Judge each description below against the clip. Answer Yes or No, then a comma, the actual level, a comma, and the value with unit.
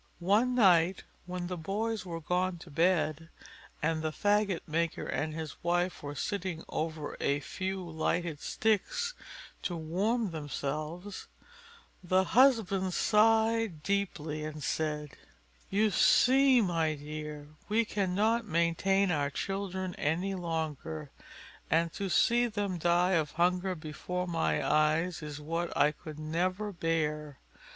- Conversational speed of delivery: No, slow, 130 wpm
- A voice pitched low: No, medium, 175 Hz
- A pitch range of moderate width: Yes, average, 4.0 semitones